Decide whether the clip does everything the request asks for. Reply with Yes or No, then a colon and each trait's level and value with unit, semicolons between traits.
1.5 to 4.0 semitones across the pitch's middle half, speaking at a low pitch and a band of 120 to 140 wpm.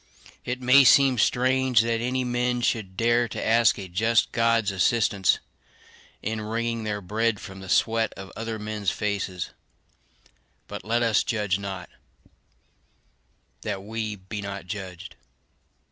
Yes: average, 2.9 semitones; low, 110 Hz; slow, 135 wpm